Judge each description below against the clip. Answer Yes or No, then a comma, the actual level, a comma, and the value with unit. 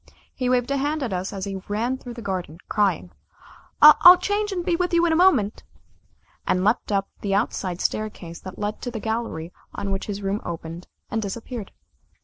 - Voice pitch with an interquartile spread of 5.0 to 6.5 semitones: Yes, average, 5.3 semitones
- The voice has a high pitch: Yes, high, 215 Hz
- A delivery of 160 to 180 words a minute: No, average, 195 wpm